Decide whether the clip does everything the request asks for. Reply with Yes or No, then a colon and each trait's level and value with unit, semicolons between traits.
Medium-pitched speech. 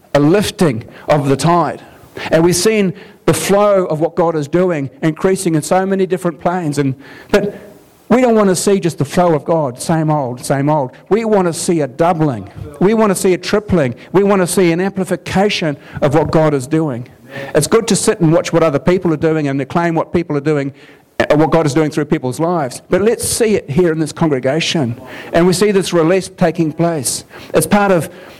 Yes: medium, 165 Hz